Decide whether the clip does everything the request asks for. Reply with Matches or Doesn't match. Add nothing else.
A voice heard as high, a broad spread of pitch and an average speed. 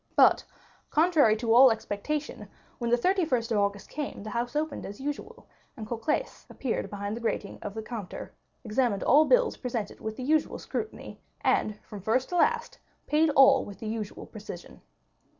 Matches